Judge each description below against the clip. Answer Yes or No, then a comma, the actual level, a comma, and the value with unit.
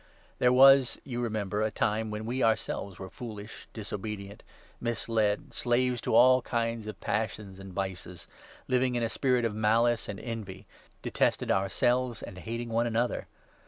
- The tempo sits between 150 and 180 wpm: Yes, average, 160 wpm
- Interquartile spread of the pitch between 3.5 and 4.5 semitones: No, average, 2.7 semitones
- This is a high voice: No, low, 115 Hz